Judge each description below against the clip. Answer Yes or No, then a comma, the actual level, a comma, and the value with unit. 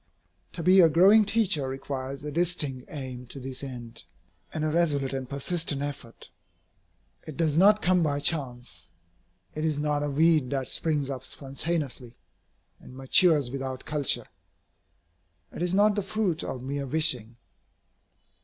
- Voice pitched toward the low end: No, medium, 145 Hz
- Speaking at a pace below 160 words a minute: Yes, average, 145 wpm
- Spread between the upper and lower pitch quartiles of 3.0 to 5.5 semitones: Yes, average, 4.0 semitones